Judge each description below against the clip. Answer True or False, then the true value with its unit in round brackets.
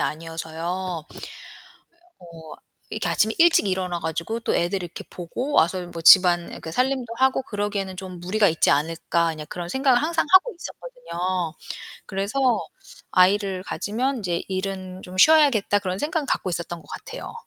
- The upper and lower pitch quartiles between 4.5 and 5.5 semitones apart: True (5.2 semitones)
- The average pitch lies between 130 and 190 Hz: True (185 Hz)